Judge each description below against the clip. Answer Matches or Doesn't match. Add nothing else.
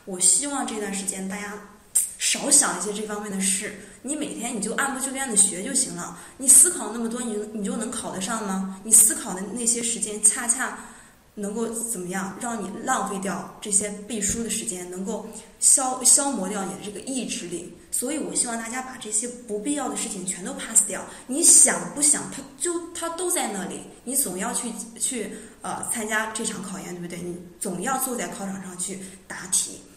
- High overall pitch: Matches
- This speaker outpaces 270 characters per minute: Matches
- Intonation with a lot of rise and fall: Doesn't match